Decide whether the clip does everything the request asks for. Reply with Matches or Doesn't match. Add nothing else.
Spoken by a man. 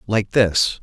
Matches